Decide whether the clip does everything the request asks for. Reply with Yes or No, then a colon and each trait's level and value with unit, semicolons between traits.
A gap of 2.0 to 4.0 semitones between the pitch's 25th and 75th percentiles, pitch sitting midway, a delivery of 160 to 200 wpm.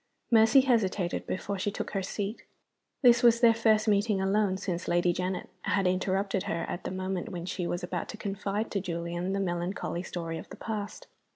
No: average, 3.0 semitones; high, 195 Hz; average, 190 wpm